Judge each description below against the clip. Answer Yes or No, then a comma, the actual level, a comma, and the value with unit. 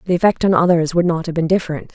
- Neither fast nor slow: No, fast, 275 wpm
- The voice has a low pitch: No, medium, 170 Hz